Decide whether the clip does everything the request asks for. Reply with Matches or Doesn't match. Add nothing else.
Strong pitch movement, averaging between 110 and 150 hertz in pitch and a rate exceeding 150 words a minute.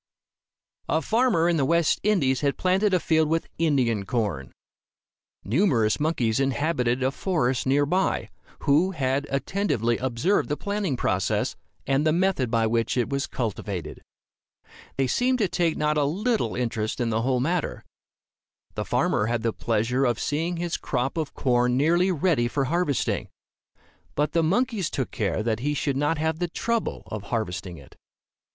Matches